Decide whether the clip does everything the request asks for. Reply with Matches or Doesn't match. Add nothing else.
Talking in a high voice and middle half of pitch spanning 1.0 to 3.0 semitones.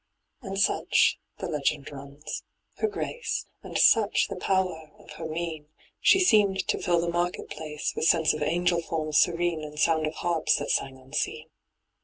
Doesn't match